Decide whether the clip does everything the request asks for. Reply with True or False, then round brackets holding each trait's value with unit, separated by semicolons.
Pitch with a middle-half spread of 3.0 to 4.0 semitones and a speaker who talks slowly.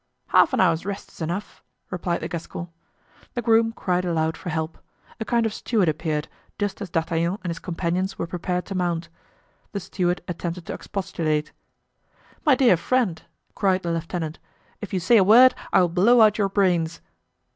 False (3.4 semitones; 180 wpm)